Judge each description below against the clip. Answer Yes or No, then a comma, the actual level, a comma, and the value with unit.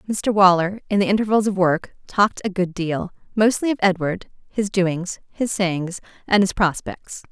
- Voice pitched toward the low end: No, high, 190 Hz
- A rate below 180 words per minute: Yes, average, 170 wpm